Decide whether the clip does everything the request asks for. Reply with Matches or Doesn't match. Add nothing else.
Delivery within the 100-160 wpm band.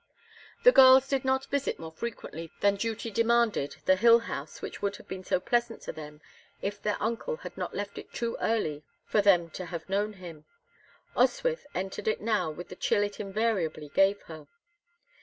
Doesn't match